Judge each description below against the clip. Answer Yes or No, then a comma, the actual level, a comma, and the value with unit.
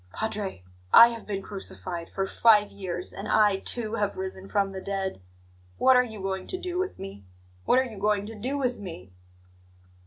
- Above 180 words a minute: Yes, average, 190 wpm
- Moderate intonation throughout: Yes, average, 3.2 semitones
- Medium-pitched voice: No, high, 205 Hz